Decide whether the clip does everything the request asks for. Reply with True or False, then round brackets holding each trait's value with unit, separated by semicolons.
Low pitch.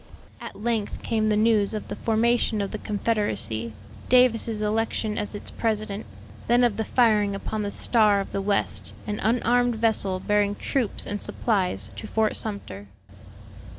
False (215 Hz)